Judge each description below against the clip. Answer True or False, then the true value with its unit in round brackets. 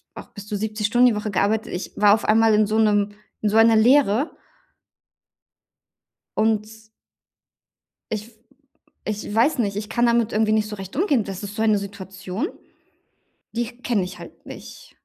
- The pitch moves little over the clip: True (1.9 semitones)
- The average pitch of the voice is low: False (215 Hz)